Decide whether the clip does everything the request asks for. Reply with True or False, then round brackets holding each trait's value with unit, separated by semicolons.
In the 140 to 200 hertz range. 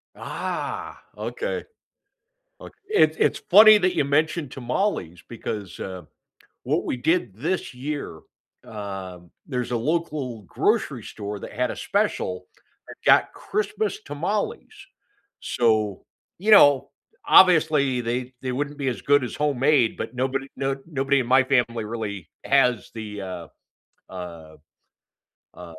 False (125 Hz)